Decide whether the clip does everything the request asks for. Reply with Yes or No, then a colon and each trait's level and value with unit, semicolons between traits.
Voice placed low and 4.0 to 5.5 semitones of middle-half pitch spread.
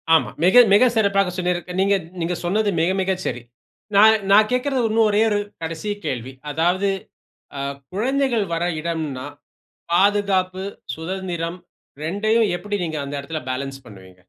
No: medium, 185 Hz; average, 4.3 semitones